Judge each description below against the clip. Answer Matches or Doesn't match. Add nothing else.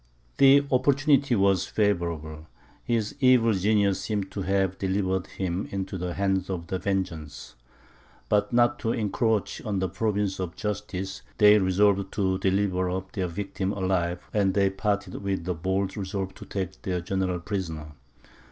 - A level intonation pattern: Matches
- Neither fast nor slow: Matches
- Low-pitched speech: Matches